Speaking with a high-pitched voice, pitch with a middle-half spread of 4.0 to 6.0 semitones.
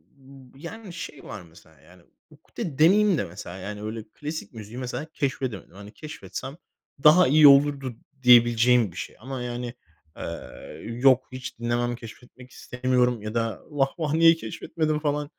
No: low, 125 Hz; average, 4.5 semitones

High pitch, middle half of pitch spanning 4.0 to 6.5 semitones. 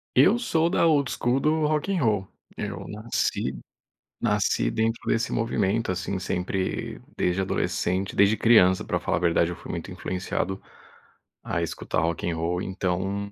No: low, 100 Hz; average, 4.4 semitones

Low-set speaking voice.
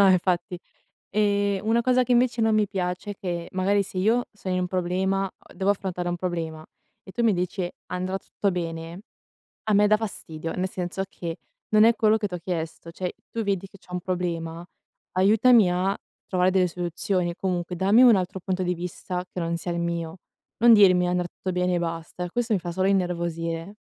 No: medium, 185 Hz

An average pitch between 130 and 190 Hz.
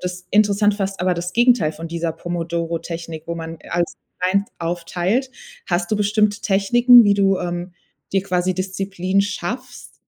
Yes: medium, 185 Hz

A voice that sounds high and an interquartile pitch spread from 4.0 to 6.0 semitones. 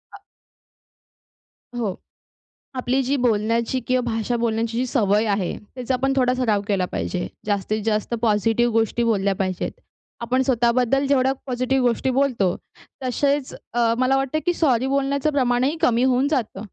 No: high, 245 Hz; average, 3.0 semitones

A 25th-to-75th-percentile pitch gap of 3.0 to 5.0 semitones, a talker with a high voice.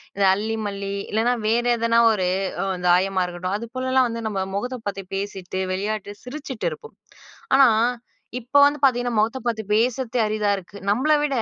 Yes: average, 4.0 semitones; high, 220 Hz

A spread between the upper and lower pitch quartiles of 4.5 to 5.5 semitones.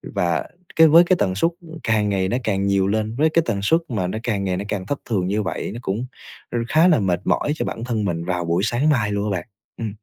No: average, 4.1 semitones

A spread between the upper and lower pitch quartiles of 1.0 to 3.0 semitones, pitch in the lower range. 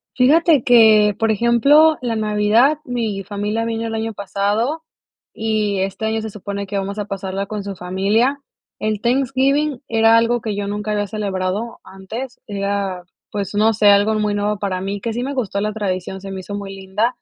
No: narrow, 2.6 semitones; high, 210 Hz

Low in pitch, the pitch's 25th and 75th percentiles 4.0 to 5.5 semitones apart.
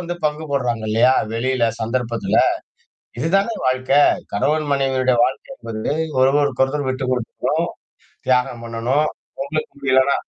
No: low, 130 Hz; average, 2.9 semitones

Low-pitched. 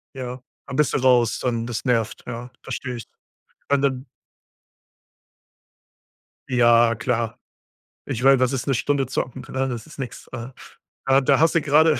Yes: low, 125 Hz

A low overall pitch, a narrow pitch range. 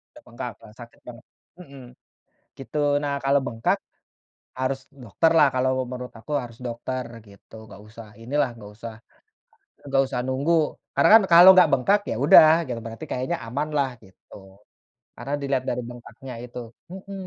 No: low, 130 Hz; average, 3.3 semitones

